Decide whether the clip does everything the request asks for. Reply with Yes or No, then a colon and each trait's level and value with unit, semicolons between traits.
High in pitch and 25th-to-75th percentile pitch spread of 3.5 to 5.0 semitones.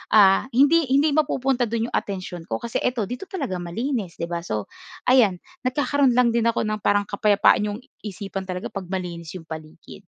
No: high, 210 Hz; wide, 5.4 semitones